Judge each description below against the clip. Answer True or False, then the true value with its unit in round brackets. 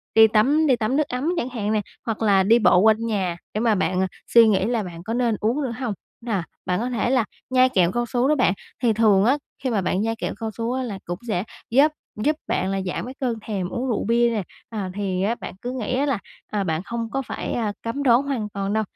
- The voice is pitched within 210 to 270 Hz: True (225 Hz)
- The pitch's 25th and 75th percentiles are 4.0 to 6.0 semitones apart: False (3.6 semitones)